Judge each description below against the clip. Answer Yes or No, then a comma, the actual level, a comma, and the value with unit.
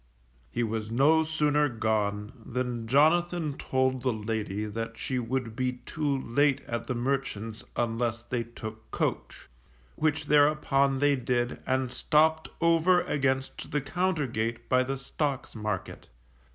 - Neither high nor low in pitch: No, low, 130 Hz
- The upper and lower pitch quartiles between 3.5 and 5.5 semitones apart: Yes, average, 4.3 semitones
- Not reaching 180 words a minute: Yes, average, 140 wpm